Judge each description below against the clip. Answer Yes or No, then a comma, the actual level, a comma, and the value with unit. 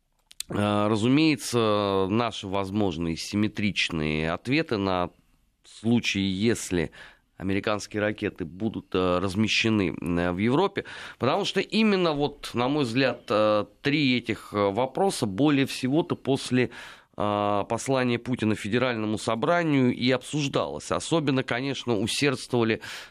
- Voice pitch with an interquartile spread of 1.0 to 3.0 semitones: No, average, 4.6 semitones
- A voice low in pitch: Yes, low, 110 Hz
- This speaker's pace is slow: Yes, slow, 95 wpm